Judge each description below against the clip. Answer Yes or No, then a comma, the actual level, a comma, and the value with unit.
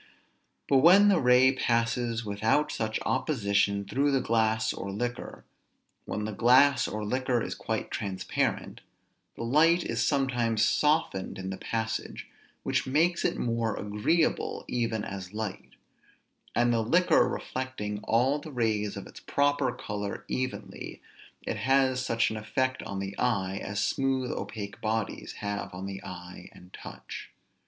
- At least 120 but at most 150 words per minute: Yes, average, 145 wpm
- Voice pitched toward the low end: Yes, low, 115 Hz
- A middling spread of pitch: Yes, average, 4.1 semitones